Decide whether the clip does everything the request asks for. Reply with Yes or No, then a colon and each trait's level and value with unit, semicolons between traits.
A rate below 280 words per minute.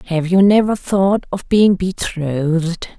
Yes: average, 140 wpm